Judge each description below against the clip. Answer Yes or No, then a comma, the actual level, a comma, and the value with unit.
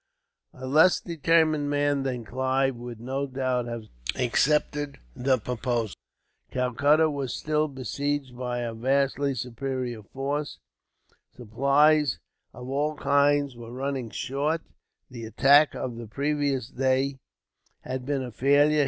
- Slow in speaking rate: Yes, slow, 125 wpm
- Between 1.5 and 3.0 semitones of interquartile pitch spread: Yes, narrow, 2.6 semitones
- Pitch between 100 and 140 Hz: Yes, low, 135 Hz